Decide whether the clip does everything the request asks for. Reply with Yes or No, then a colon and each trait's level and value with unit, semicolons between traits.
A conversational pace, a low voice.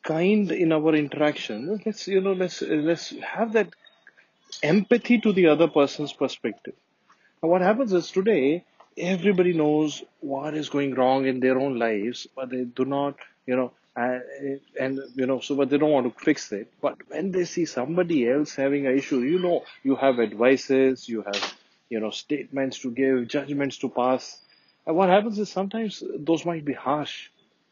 No: average, 180 wpm; medium, 145 Hz